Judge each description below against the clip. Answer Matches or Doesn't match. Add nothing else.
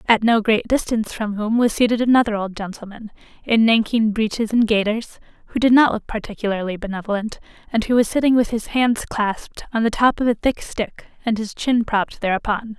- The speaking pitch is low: Doesn't match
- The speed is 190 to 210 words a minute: Matches